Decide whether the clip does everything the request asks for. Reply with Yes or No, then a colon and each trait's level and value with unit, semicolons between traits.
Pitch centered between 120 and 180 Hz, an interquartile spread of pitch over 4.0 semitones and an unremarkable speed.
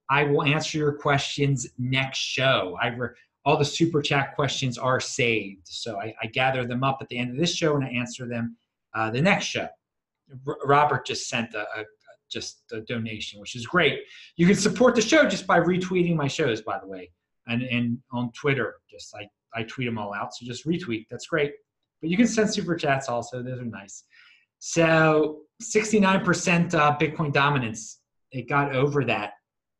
Yes: low, 135 Hz; average, 5.0 semitones; average, 195 wpm